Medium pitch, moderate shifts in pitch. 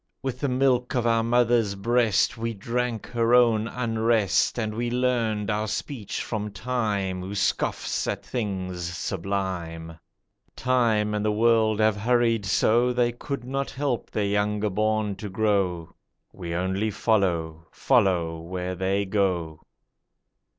No: low, 110 Hz; average, 3.6 semitones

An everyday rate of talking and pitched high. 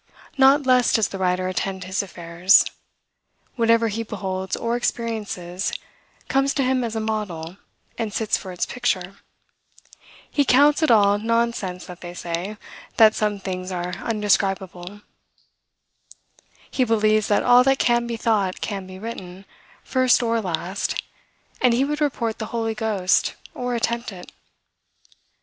Yes: average, 145 wpm; high, 215 Hz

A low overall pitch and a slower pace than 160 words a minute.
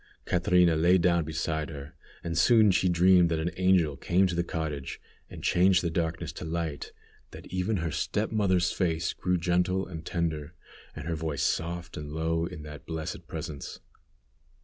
No: very low, 85 Hz; average, 170 wpm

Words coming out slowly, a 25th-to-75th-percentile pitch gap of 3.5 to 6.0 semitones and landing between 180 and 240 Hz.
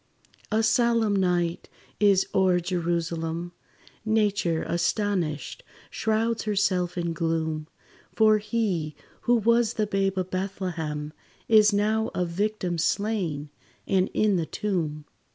Yes: slow, 115 wpm; average, 4.1 semitones; high, 190 Hz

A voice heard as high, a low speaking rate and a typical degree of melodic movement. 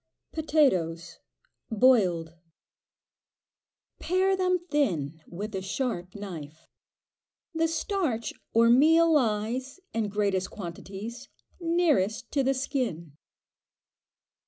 No: high, 230 Hz; slow, 85 wpm; wide, 7.9 semitones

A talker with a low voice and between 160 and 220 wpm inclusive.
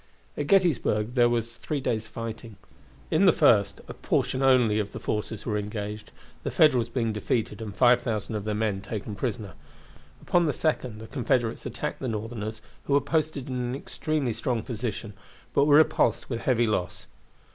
Yes: low, 115 Hz; average, 175 wpm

